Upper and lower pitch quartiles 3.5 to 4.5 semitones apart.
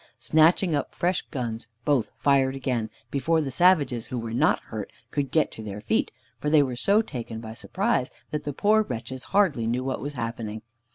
No: average, 5.0 semitones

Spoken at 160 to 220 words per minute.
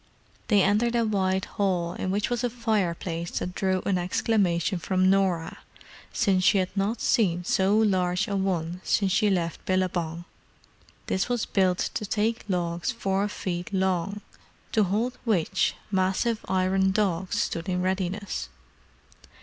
No: average, 145 wpm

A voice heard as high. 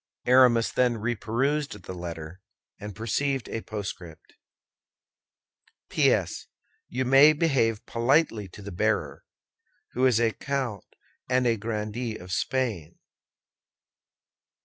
No: low, 115 Hz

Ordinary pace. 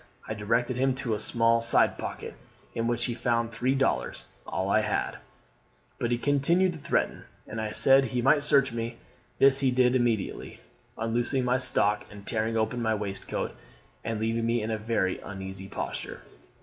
Yes: average, 175 wpm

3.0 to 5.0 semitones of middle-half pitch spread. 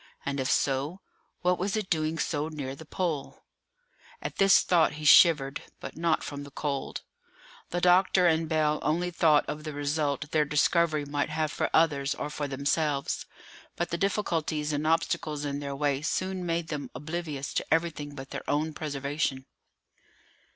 No: narrow, 2.5 semitones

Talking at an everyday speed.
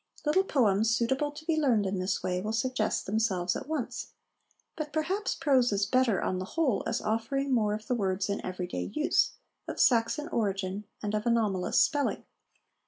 Yes: average, 175 wpm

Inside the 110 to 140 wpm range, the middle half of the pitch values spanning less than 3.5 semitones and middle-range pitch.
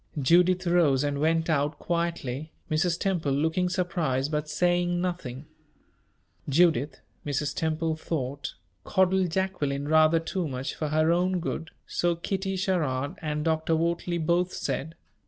Yes: slow, 135 wpm; average, 3.1 semitones; medium, 160 Hz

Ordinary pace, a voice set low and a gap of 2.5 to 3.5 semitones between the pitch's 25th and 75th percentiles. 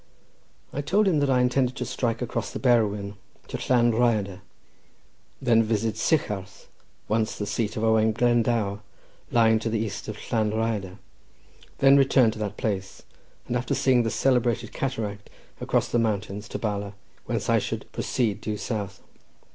Yes: average, 155 wpm; low, 110 Hz; average, 2.8 semitones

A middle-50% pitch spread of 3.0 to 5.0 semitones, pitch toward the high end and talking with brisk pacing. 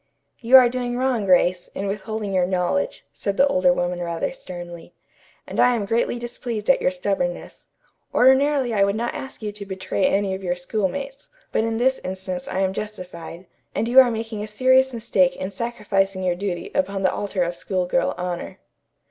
No: average, 4.4 semitones; high, 200 Hz; average, 190 wpm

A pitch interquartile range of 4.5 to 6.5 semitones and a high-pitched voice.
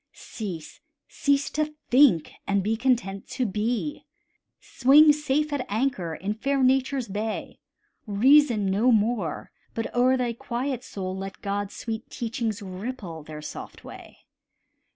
Yes: average, 4.9 semitones; high, 230 Hz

